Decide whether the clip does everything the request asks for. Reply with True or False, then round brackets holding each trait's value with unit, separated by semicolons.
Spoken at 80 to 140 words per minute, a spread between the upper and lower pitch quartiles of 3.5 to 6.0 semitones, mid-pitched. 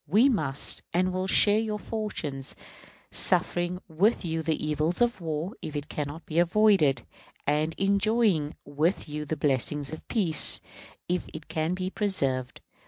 False (155 wpm; 4.6 semitones; 165 Hz)